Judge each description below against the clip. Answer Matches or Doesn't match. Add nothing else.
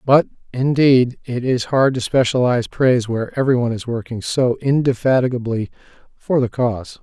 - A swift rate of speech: Doesn't match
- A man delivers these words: Matches